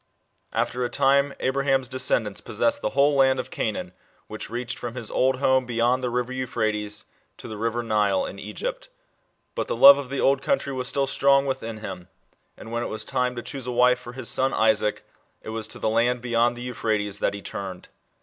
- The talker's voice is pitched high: No, low, 125 Hz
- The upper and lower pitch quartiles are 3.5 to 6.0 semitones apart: No, average, 3.1 semitones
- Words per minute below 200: No, fast, 205 wpm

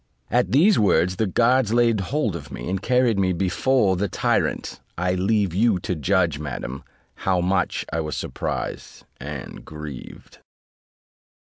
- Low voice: Yes, very low, 95 Hz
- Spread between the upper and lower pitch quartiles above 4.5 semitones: Yes, average, 5.1 semitones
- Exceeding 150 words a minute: No, average, 145 wpm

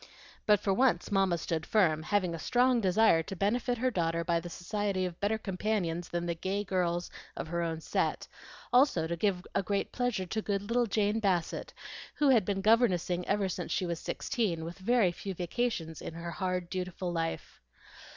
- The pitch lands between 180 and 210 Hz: Yes, medium, 185 Hz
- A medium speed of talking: Yes, average, 190 wpm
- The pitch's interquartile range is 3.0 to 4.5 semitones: Yes, average, 3.8 semitones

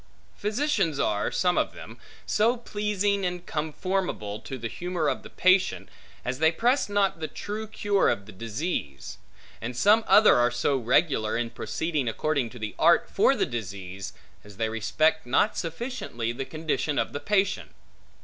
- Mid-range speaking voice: Yes, medium, 155 Hz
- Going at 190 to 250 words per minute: No, average, 160 wpm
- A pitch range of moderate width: No, wide, 9.0 semitones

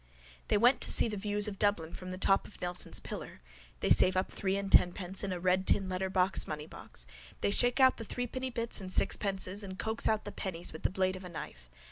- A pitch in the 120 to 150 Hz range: No, high, 190 Hz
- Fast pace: Yes, fast, 225 wpm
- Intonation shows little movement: Yes, narrow, 2.2 semitones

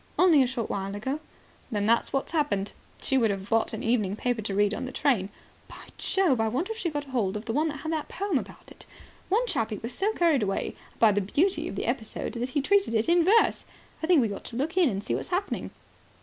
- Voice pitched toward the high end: Yes, very high, 255 Hz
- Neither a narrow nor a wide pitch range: No, wide, 7.0 semitones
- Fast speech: Yes, fast, 250 wpm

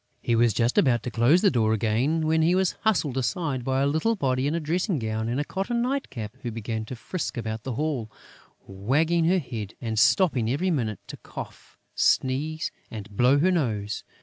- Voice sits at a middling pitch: No, low, 130 Hz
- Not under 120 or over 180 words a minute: No, average, 200 wpm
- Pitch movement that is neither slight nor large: No, wide, 6.2 semitones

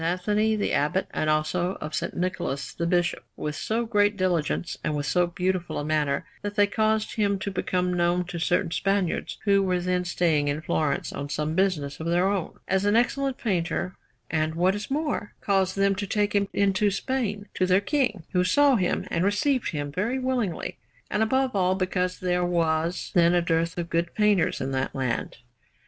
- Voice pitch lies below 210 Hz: Yes, medium, 185 Hz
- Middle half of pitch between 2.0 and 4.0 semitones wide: Yes, average, 3.4 semitones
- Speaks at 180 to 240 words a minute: Yes, average, 195 wpm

